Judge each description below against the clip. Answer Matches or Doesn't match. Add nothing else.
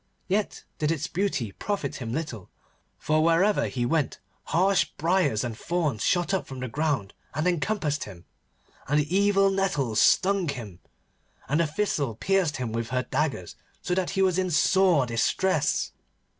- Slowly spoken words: Doesn't match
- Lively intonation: Matches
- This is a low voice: Doesn't match